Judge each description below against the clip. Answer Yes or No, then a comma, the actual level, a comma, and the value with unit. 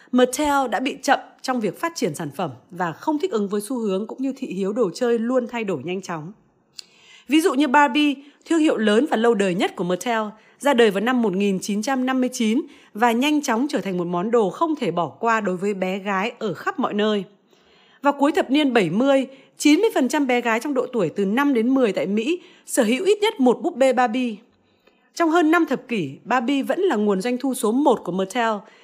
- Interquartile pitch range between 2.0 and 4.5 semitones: No, average, 5.3 semitones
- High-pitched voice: Yes, high, 245 Hz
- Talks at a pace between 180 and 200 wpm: No, average, 220 wpm